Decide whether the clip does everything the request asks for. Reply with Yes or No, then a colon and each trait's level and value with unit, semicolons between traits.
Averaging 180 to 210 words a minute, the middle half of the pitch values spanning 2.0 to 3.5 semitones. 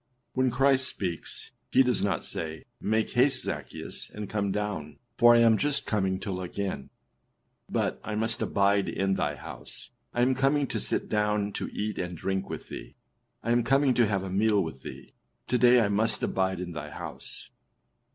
No: average, 190 wpm; average, 4.2 semitones